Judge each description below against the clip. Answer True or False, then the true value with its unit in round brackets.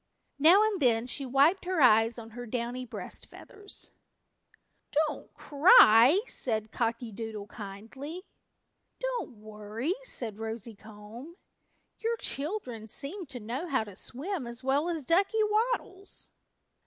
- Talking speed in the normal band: False (130 wpm)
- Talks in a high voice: True (255 Hz)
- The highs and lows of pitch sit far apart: True (7.7 semitones)